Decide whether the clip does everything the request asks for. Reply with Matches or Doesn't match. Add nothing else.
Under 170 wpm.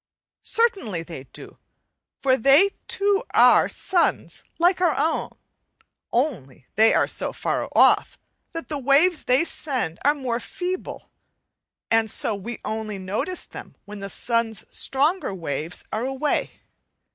Matches